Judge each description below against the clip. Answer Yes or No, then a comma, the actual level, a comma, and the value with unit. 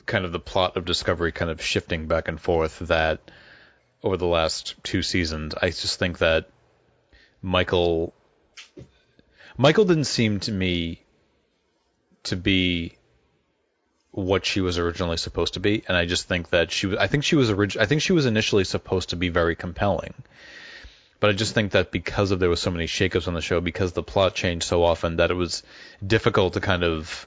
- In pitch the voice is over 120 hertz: No, very low, 90 Hz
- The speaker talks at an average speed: Yes, average, 190 wpm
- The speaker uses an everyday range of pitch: Yes, average, 3.3 semitones